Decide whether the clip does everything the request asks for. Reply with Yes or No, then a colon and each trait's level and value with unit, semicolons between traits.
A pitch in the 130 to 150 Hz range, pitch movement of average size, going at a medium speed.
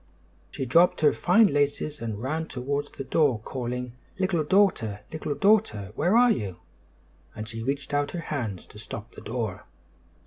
No: medium, 140 Hz; wide, 6.0 semitones; average, 165 wpm